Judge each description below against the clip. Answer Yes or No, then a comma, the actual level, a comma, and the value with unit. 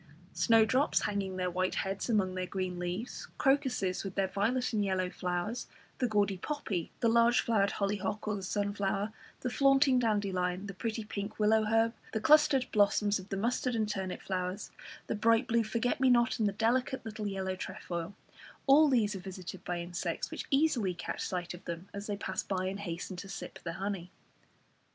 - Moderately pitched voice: No, high, 205 Hz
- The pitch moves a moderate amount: Yes, average, 3.5 semitones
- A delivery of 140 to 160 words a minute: No, average, 185 wpm